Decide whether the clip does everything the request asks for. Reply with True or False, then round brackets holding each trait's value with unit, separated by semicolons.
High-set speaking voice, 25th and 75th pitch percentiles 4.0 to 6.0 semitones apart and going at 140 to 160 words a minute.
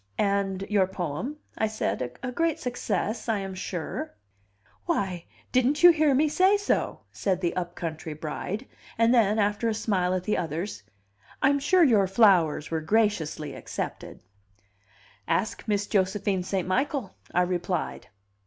True (200 Hz; 5.1 semitones; 145 wpm)